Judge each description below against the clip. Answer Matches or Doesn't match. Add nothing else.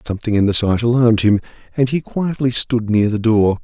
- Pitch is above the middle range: Doesn't match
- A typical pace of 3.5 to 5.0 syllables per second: Doesn't match